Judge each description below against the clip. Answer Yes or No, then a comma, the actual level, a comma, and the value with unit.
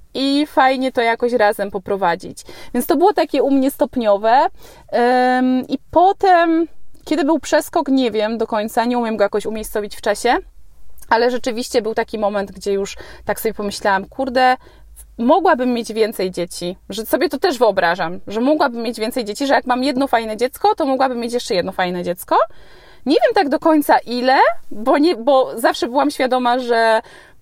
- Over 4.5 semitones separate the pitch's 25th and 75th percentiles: Yes, average, 5.1 semitones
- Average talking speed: No, fast, 175 wpm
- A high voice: Yes, high, 245 Hz